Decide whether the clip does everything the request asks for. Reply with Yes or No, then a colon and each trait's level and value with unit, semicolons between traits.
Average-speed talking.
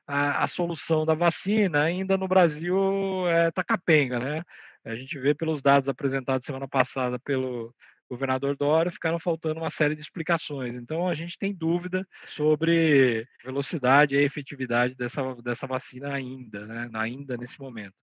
Yes: average, 145 wpm